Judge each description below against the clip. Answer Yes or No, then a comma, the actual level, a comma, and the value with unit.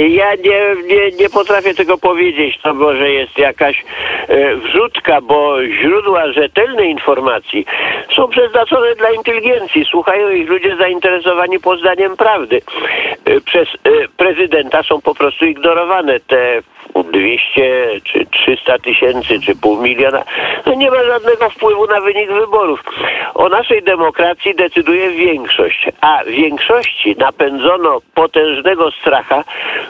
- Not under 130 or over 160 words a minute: No, average, 115 wpm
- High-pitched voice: Yes, high, 200 Hz